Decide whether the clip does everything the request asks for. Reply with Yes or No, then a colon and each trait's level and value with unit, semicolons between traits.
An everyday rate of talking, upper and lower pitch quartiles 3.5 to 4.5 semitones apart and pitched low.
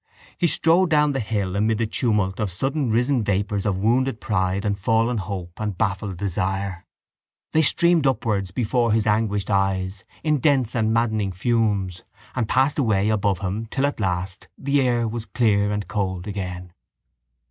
Yes: average, 160 wpm; average, 3.8 semitones; low, 105 Hz